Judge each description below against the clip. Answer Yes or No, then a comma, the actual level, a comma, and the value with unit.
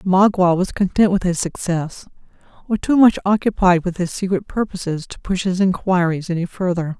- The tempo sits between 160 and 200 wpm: Yes, average, 170 wpm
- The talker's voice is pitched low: No, medium, 185 Hz